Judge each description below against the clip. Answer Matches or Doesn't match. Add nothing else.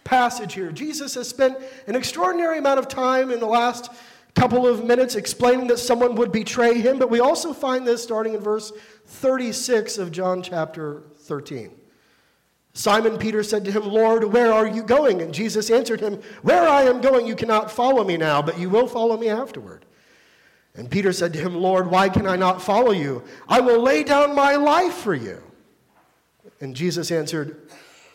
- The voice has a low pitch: Doesn't match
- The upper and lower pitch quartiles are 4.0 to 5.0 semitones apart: Matches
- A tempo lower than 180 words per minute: Doesn't match